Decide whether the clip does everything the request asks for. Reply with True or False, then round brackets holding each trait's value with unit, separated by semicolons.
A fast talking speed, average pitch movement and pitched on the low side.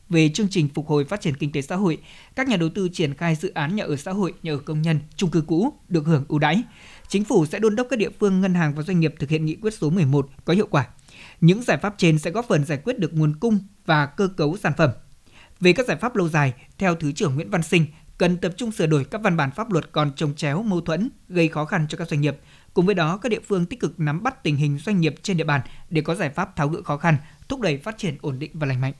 False (290 wpm; 4.2 semitones; 165 Hz)